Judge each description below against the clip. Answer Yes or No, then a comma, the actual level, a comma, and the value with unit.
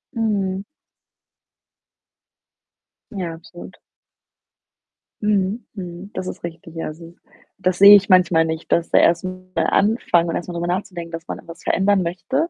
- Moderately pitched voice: Yes, medium, 180 Hz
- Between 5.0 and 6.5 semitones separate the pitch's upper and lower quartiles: No, average, 2.7 semitones